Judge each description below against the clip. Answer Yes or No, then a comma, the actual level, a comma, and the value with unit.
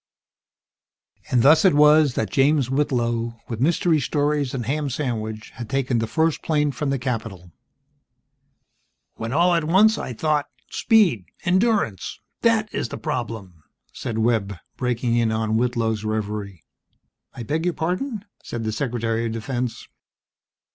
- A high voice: No, low, 125 Hz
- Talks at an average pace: Yes, average, 145 wpm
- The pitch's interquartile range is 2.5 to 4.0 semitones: No, average, 5.3 semitones